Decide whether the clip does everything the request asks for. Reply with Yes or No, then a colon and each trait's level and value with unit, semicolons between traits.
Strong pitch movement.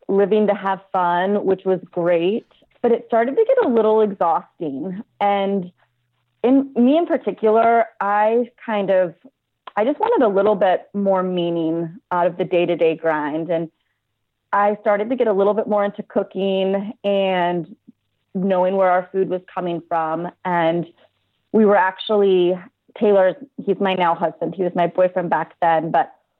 No: average, 3.4 semitones